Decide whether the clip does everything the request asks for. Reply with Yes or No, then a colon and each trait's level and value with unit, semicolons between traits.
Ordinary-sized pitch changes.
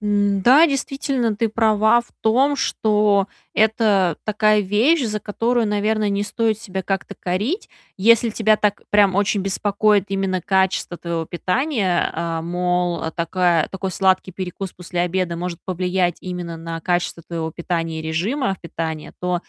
Yes: average, 3.3 semitones